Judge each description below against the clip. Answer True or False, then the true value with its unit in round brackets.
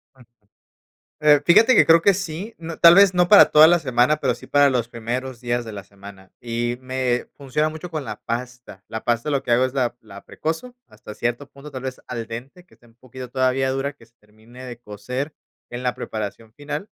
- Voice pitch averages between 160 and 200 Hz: False (130 Hz)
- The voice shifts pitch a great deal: False (4.3 semitones)